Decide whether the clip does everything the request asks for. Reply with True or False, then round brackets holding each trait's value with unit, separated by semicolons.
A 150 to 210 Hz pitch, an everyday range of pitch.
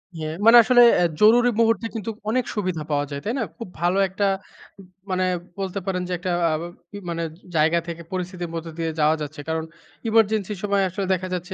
True (185 Hz; 4.2 semitones)